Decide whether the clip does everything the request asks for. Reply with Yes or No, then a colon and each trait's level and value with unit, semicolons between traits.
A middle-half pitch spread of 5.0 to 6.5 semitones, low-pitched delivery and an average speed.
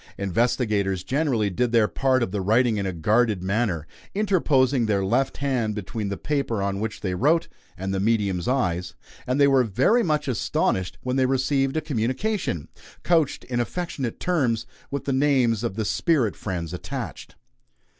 Yes: wide, 5.5 semitones; low, 120 Hz; average, 165 wpm